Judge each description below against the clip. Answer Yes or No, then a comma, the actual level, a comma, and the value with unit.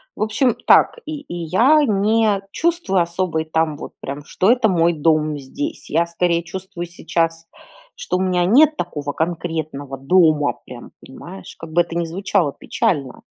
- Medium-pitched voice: Yes, medium, 170 Hz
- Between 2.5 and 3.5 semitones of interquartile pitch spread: No, average, 4.1 semitones